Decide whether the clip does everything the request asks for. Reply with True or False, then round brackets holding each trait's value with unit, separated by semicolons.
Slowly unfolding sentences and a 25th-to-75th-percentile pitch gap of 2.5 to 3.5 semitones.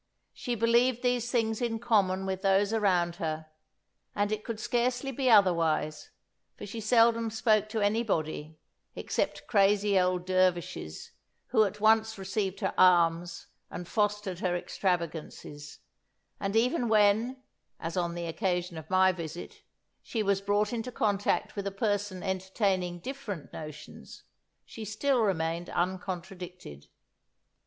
False (130 wpm; 3.9 semitones)